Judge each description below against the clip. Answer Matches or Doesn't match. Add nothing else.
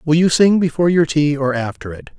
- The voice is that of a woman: Doesn't match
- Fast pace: Matches